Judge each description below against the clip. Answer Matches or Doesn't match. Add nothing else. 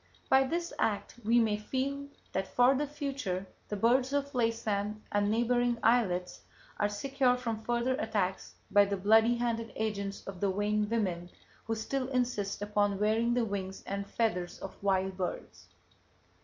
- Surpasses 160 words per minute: Doesn't match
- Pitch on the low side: Doesn't match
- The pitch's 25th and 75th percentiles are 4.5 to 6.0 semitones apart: Doesn't match